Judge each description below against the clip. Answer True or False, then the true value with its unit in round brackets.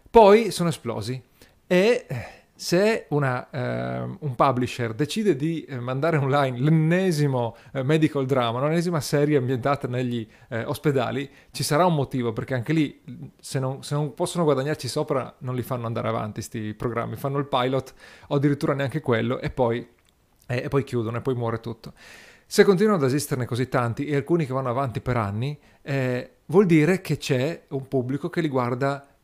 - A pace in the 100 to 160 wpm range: False (170 wpm)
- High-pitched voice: False (135 Hz)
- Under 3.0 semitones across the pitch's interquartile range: False (3.5 semitones)